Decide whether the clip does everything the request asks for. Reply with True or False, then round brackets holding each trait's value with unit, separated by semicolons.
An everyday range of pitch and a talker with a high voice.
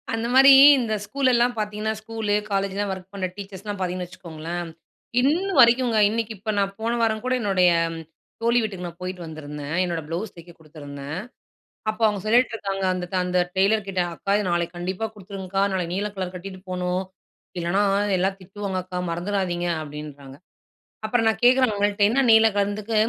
True (3.4 semitones; 195 Hz)